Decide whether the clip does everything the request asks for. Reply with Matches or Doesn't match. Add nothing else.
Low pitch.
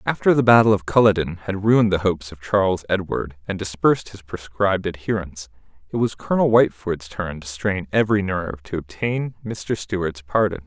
Matches